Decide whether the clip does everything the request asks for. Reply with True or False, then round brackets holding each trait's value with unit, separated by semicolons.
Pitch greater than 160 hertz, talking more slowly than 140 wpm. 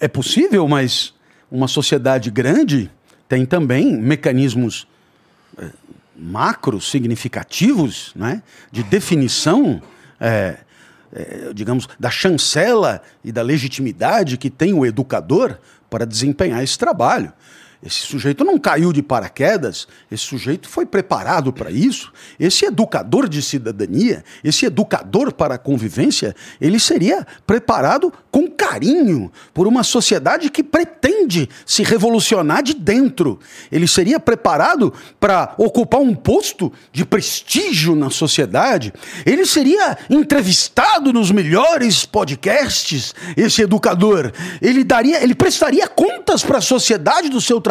True (190 Hz; 120 wpm)